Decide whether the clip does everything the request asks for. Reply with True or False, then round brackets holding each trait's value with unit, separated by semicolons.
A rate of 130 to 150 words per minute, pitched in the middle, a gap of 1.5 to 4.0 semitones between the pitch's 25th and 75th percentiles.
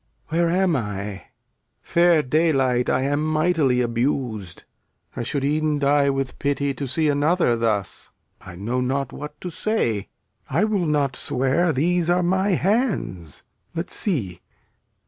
False (140 wpm; 145 Hz; 5.2 semitones)